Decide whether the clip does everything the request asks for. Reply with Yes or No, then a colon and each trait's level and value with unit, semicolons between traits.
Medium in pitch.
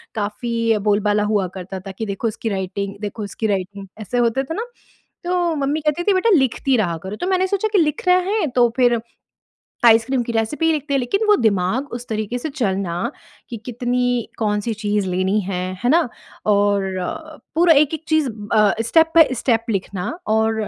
No: high, 230 Hz